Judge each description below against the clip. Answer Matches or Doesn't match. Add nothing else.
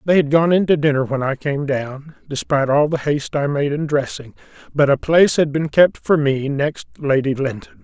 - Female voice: Doesn't match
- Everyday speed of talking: Doesn't match